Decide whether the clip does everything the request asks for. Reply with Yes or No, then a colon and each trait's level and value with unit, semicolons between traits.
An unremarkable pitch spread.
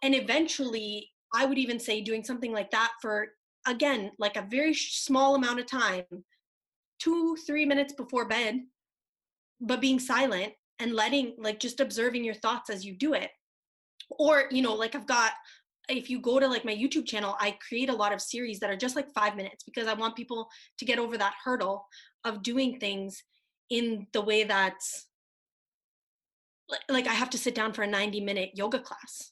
Yes: average, 3.8 semitones